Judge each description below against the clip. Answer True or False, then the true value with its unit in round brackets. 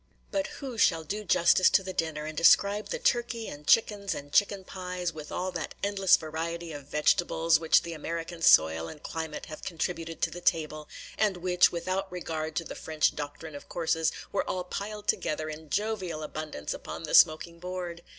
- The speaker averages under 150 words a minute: False (185 wpm)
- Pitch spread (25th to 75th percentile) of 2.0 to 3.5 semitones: True (3.2 semitones)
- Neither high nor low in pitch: True (170 Hz)